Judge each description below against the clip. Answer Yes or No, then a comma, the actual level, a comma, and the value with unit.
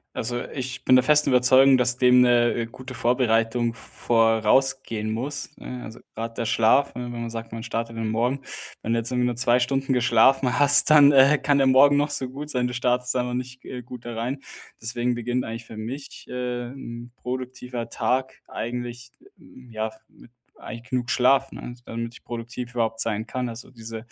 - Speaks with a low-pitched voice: Yes, low, 125 Hz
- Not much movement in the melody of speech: Yes, narrow, 1.9 semitones